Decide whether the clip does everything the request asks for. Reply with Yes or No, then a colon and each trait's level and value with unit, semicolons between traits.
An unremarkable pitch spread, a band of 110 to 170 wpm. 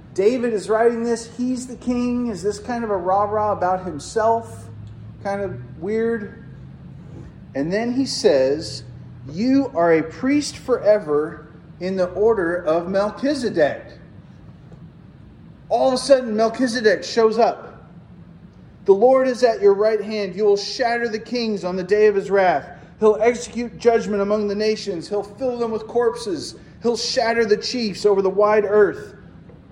Yes: average, 3.2 semitones; average, 155 wpm